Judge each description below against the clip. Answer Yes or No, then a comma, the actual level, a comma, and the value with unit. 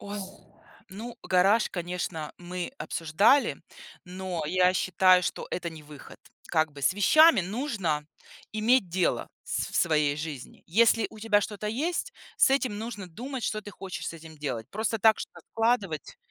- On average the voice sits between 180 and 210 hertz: Yes, high, 190 Hz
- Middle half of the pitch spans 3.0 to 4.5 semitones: No, average, 5.2 semitones